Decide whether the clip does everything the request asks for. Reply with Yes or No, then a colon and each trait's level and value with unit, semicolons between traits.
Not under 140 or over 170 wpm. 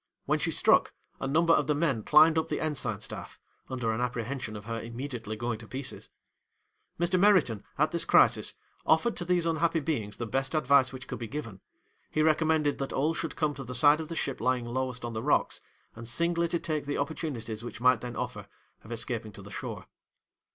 No: fast, 205 wpm